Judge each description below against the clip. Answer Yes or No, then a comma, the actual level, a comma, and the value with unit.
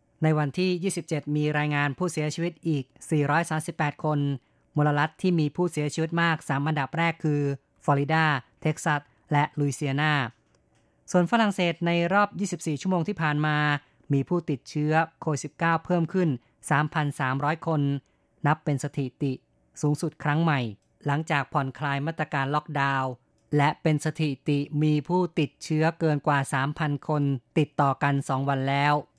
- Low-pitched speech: No, medium, 150 Hz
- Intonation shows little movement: Yes, narrow, 2.2 semitones